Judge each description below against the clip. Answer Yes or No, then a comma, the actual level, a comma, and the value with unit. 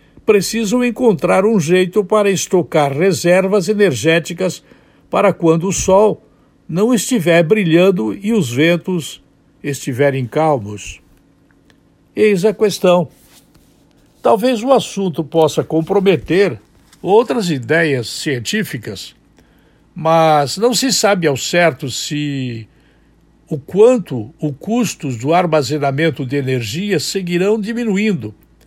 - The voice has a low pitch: No, medium, 170 Hz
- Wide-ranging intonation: Yes, wide, 6.0 semitones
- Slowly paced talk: Yes, slow, 100 wpm